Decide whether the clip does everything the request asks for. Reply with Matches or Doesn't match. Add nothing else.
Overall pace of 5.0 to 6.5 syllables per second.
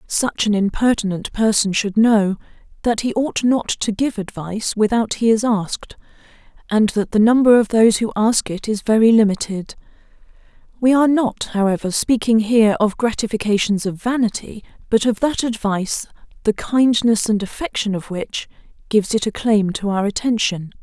Matches